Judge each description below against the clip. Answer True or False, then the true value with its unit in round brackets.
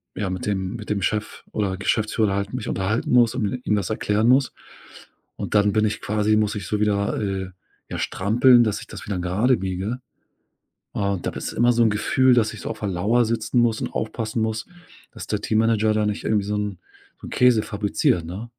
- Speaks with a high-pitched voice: False (105 Hz)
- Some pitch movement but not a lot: False (2.1 semitones)